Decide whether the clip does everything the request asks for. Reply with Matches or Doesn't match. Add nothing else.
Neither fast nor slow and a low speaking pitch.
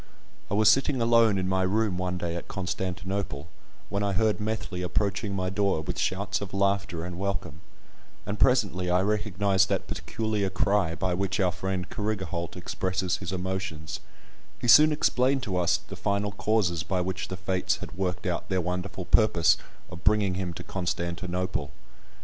Matches